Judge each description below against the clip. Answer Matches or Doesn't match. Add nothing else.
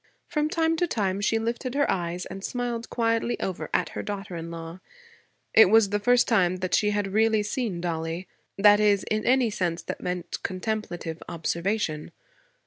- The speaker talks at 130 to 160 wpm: Doesn't match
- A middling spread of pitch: Matches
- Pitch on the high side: Matches